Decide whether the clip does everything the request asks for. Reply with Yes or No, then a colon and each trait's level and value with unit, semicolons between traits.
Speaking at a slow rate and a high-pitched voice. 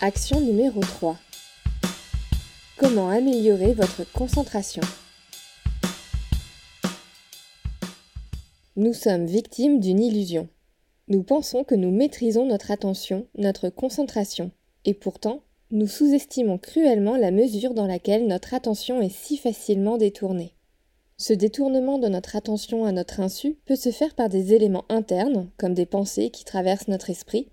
Yes: slow, 125 wpm; high, 215 Hz